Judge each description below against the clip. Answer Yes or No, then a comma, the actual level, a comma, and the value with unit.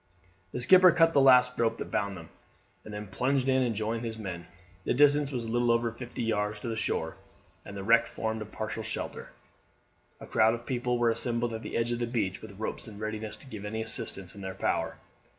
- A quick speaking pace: Yes, fast, 220 wpm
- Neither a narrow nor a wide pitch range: No, narrow, 2.3 semitones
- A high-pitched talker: No, low, 115 Hz